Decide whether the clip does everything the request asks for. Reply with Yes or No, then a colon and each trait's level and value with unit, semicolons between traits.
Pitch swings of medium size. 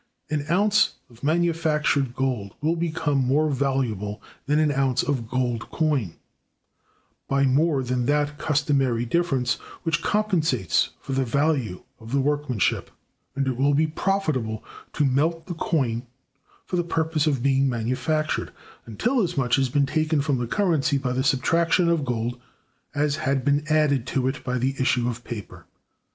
Yes: average, 3.7 semitones